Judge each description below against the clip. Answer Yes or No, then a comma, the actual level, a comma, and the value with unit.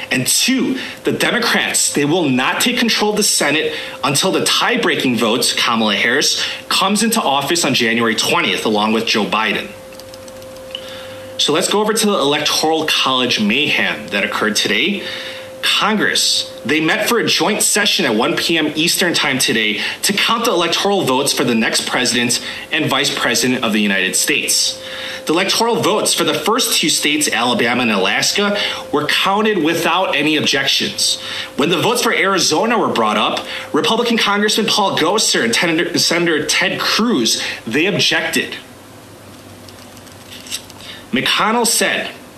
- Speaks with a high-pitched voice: No, medium, 170 Hz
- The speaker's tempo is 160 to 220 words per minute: No, average, 150 wpm